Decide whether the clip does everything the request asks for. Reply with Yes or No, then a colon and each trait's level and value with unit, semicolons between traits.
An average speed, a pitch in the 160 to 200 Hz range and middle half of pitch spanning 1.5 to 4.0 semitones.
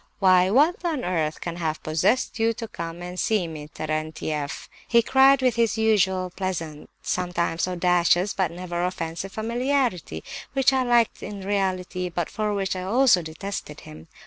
No: average, 160 wpm; medium, 185 Hz; average, 4.9 semitones